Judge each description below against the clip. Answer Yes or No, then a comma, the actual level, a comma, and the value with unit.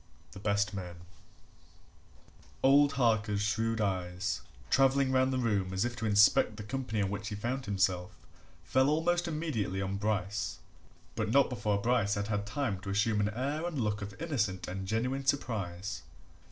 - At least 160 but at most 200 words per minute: Yes, average, 165 wpm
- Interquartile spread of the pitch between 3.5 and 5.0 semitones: Yes, average, 4.5 semitones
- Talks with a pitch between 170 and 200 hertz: No, low, 105 Hz